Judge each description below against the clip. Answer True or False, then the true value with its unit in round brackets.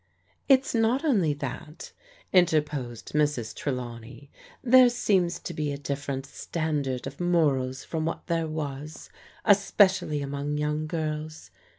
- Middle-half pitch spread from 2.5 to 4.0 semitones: True (3.6 semitones)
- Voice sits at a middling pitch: True (150 Hz)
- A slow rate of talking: True (125 wpm)